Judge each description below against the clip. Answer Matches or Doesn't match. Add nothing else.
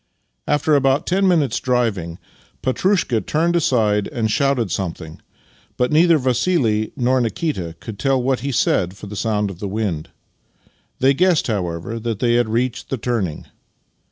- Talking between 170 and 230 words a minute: Doesn't match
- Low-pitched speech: Matches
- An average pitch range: Matches